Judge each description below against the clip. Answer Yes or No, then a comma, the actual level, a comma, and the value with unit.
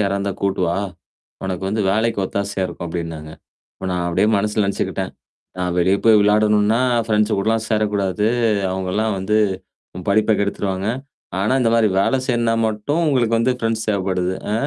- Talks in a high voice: No, low, 105 Hz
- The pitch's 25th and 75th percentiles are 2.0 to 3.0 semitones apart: Yes, narrow, 2.6 semitones